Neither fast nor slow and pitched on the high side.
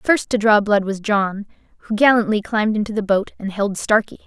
No: fast, 210 wpm; high, 210 Hz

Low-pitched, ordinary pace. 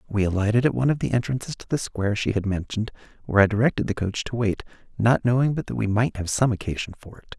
No: low, 110 Hz; fast, 250 wpm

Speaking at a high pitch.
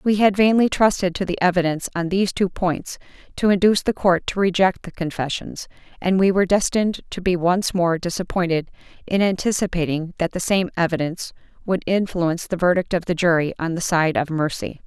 No: medium, 180 Hz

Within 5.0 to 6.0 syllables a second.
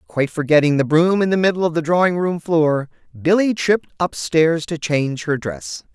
Yes: 5.2 syllables/s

